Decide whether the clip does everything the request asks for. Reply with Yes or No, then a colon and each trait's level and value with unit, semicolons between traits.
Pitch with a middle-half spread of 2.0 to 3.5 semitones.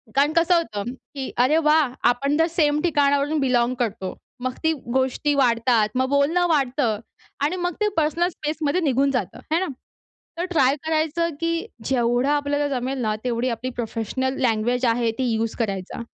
No: average, 4.1 semitones